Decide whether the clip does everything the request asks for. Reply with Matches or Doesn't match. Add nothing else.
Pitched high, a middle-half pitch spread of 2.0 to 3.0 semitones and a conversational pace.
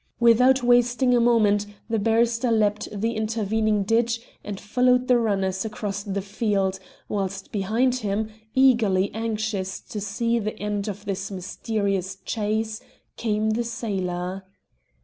Doesn't match